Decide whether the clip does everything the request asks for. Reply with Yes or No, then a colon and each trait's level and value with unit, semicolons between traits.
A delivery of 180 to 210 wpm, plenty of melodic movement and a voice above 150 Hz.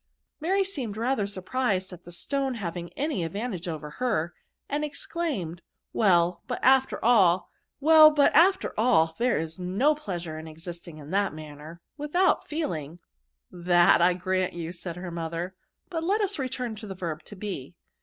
No: average, 165 wpm; wide, 7.7 semitones; high, 190 Hz